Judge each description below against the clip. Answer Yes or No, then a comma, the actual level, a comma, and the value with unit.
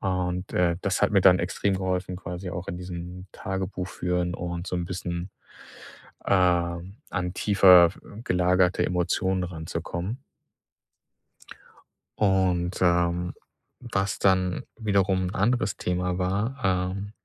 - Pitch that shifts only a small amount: Yes, narrow, 1.4 semitones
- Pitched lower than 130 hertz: Yes, very low, 90 Hz